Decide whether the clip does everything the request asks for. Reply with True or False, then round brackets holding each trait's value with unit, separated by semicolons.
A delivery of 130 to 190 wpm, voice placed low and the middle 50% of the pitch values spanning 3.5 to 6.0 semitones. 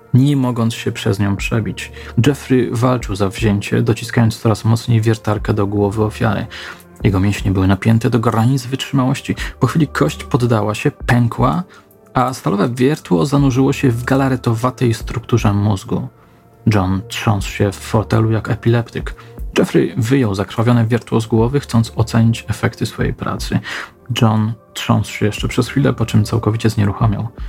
False (145 wpm; 115 Hz; 2.9 semitones)